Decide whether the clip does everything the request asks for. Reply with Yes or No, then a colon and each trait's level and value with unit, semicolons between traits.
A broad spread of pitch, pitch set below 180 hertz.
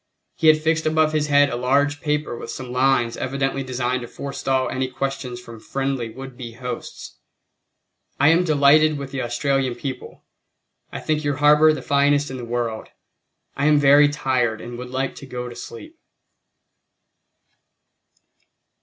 No: narrow, 2.6 semitones; low, 135 Hz